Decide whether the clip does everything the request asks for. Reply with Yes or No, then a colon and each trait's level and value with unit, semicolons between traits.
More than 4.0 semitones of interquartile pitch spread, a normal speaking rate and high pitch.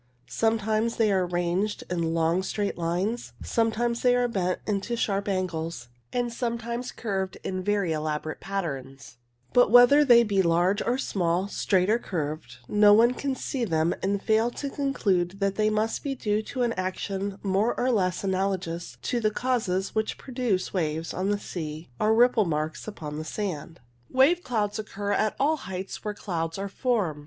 Yes: average, 4.6 semitones; average, 170 wpm; high, 200 Hz